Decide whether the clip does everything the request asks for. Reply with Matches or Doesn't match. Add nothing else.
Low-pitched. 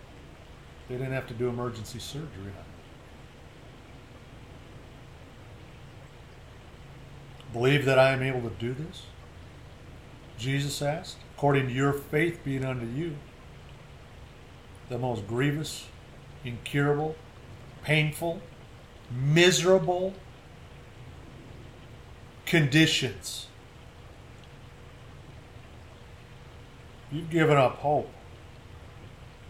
Matches